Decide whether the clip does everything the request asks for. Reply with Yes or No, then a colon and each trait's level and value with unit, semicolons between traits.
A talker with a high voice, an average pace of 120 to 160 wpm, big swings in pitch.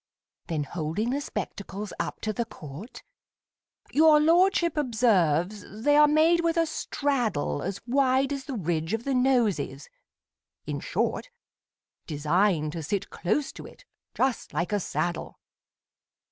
Yes: high, 225 Hz; average, 140 wpm; wide, 8.5 semitones